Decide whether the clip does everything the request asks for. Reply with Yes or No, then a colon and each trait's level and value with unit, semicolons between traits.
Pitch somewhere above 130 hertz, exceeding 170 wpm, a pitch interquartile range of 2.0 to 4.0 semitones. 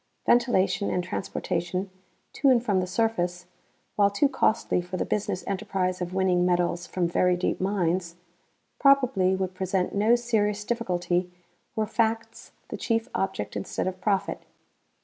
No: high, 190 Hz; average, 145 wpm; average, 3.5 semitones